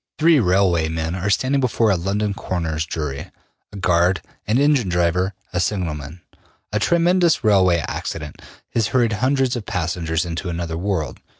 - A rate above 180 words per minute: No, average, 155 wpm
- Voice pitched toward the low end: Yes, very low, 95 Hz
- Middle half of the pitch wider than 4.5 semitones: Yes, average, 5.0 semitones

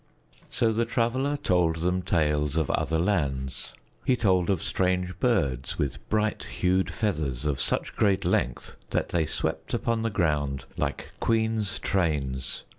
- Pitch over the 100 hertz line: No, very low, 90 Hz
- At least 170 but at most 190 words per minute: No, average, 145 wpm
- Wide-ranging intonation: Yes, wide, 6.5 semitones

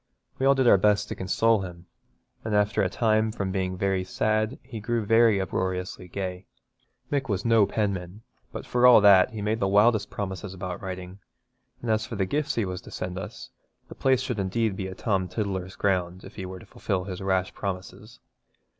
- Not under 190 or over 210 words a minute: Yes, average, 200 wpm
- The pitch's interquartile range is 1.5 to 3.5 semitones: Yes, average, 3.0 semitones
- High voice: No, low, 100 Hz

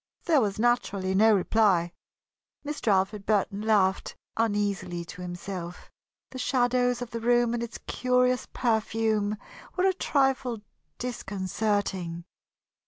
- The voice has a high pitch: Yes, high, 220 Hz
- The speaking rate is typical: No, slow, 115 wpm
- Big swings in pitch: No, average, 4.0 semitones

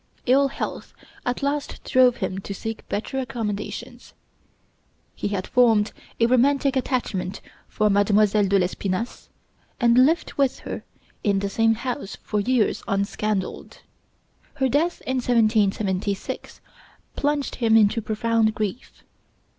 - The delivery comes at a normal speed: No, slow, 125 wpm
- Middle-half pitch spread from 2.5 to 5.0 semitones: Yes, average, 3.9 semitones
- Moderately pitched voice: No, high, 225 Hz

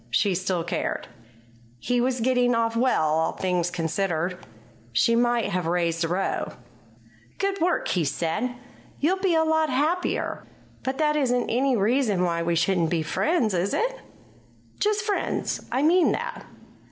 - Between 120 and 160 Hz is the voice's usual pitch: No, high, 230 Hz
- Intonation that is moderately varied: No, wide, 8.6 semitones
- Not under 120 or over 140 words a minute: No, average, 155 wpm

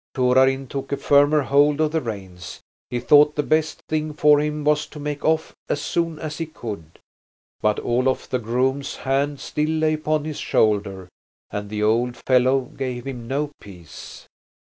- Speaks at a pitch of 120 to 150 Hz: Yes, low, 135 Hz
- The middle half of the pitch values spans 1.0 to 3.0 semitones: No, average, 3.8 semitones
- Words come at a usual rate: Yes, average, 170 wpm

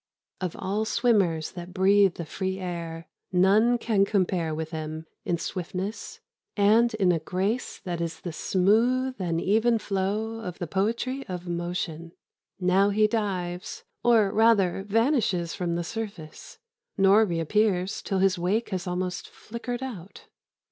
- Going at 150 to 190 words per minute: No, average, 140 wpm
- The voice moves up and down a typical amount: Yes, average, 3.8 semitones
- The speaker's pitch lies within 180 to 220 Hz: Yes, high, 190 Hz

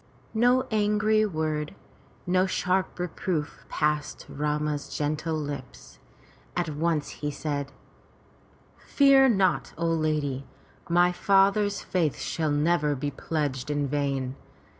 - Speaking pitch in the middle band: Yes, medium, 155 Hz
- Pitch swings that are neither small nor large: Yes, average, 4.1 semitones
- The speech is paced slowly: Yes, slow, 110 wpm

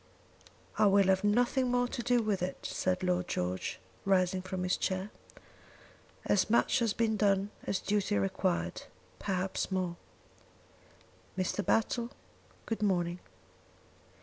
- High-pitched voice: Yes, high, 195 Hz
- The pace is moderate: No, slow, 125 wpm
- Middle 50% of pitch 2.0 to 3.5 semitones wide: Yes, average, 2.8 semitones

